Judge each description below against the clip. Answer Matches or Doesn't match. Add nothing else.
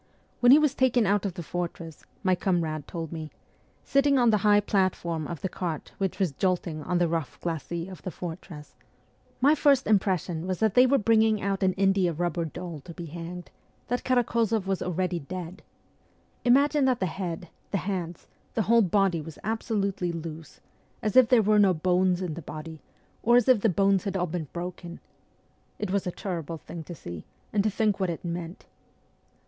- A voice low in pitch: Doesn't match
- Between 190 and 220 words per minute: Matches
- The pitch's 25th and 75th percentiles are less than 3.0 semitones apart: Doesn't match